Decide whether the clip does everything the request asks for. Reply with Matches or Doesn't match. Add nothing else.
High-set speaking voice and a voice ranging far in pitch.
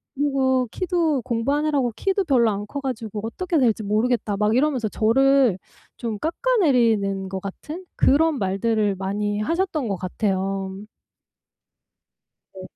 Matches